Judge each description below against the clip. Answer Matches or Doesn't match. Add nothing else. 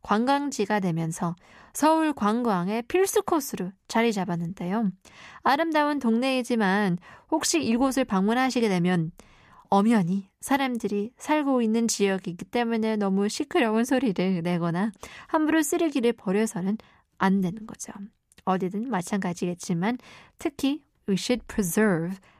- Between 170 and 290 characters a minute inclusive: Doesn't match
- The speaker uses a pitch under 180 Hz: Doesn't match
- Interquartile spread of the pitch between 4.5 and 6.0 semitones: Matches